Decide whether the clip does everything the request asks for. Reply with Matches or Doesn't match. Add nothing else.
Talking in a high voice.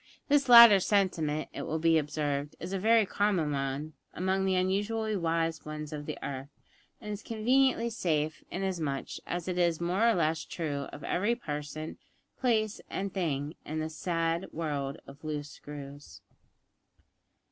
Doesn't match